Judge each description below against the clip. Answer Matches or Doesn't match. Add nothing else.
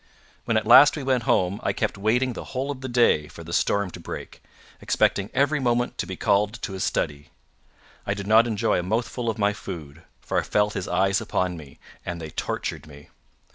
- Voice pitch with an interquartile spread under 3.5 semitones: Doesn't match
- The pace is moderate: Doesn't match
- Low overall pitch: Matches